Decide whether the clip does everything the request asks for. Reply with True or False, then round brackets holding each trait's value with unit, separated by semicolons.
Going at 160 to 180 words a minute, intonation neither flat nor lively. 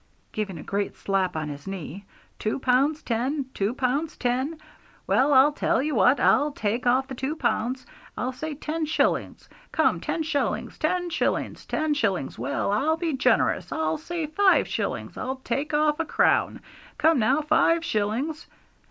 False (165 wpm; 5.9 semitones)